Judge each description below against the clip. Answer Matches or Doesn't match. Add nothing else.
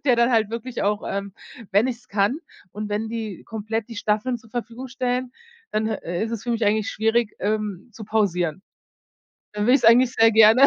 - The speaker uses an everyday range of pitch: Doesn't match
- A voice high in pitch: Matches